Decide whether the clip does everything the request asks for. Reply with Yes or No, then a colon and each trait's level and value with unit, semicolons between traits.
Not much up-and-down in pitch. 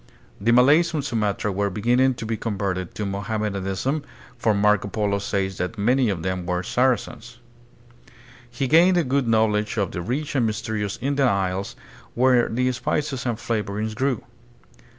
No: average, 4.1 semitones